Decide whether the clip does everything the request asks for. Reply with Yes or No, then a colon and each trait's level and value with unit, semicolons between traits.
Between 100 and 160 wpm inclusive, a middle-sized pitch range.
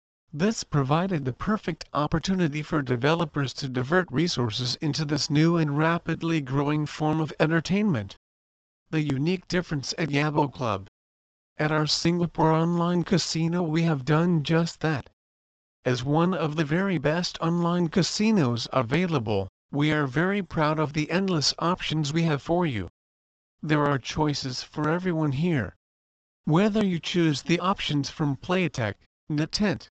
Yes: average, 140 wpm; average, 4.2 semitones